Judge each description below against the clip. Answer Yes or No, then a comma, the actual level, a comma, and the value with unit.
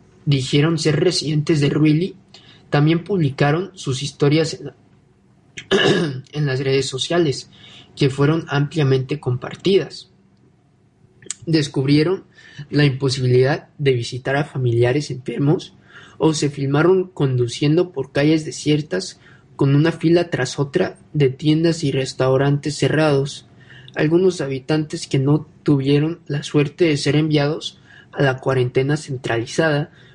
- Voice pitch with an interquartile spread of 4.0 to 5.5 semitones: No, average, 3.1 semitones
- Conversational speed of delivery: No, slow, 115 wpm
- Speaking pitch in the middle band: Yes, medium, 145 Hz